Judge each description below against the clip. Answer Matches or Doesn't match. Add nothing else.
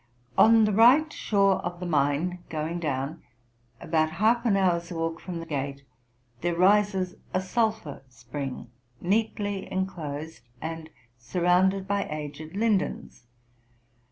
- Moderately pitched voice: Matches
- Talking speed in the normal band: Doesn't match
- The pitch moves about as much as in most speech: Matches